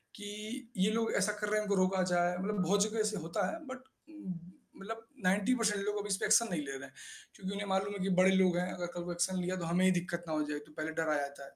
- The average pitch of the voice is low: No, high, 190 Hz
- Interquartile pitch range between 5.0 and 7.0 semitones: No, average, 3.2 semitones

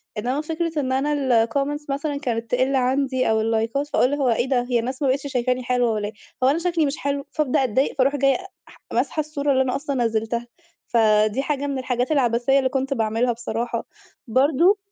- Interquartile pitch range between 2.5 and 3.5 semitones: Yes, average, 3.0 semitones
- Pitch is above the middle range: Yes, very high, 260 Hz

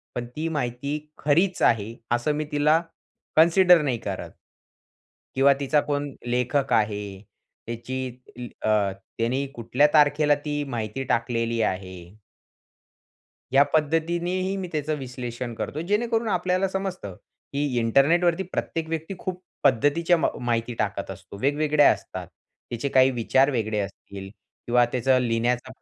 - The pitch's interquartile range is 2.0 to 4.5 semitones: No, average, 5.2 semitones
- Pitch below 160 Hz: Yes, low, 135 Hz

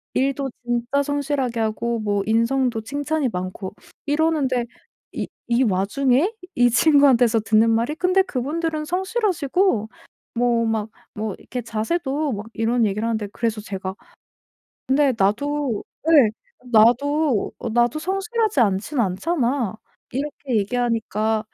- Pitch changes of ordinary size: Yes, average, 4.7 semitones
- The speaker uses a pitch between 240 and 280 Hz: Yes, high, 245 Hz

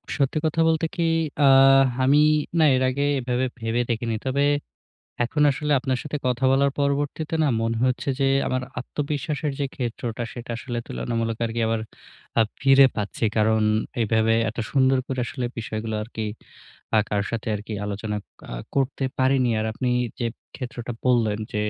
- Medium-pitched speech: No, low, 125 Hz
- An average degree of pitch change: Yes, average, 3.5 semitones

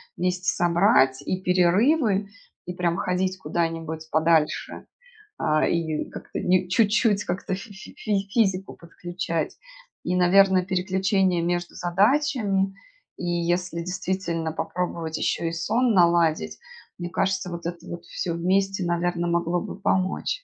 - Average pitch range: No, narrow, 2.1 semitones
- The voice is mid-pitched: Yes, medium, 180 Hz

